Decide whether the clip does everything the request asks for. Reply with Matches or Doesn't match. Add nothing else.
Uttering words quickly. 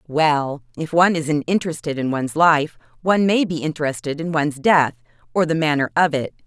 Doesn't match